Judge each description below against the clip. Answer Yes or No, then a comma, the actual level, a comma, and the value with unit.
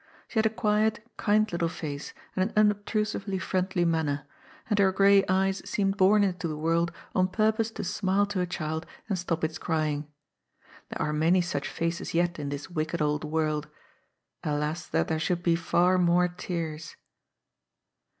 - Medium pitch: Yes, medium, 175 Hz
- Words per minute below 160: No, average, 170 wpm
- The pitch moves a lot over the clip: No, average, 3.7 semitones